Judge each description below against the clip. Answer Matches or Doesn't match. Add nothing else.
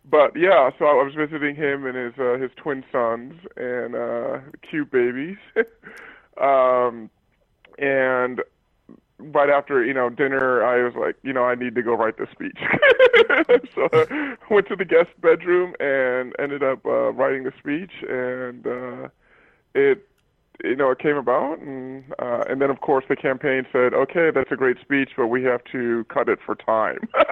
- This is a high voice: Doesn't match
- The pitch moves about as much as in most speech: Doesn't match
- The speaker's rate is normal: Matches